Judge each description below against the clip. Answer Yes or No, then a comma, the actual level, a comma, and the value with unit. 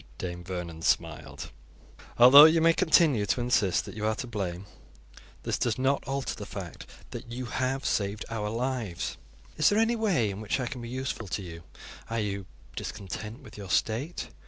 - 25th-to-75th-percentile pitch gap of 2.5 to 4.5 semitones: No, average, 5.0 semitones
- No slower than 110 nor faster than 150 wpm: No, average, 180 wpm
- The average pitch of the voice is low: Yes, low, 115 Hz